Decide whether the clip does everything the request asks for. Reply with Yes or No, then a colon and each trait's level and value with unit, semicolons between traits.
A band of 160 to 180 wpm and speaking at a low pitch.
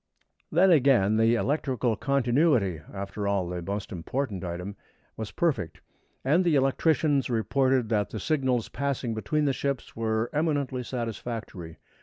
No: slow, 135 wpm; low, 120 Hz